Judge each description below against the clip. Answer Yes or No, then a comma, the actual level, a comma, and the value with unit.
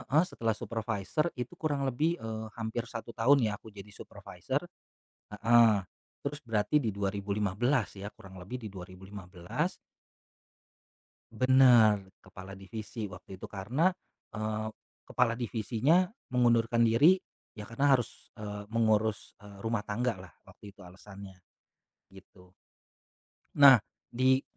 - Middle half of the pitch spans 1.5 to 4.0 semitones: Yes, average, 3.5 semitones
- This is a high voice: No, low, 110 Hz